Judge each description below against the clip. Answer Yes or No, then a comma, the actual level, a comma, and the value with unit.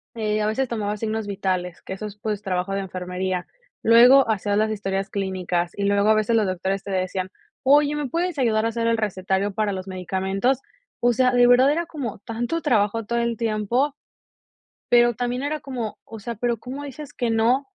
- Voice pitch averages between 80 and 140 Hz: No, high, 215 Hz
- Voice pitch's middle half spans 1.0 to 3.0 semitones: No, average, 3.8 semitones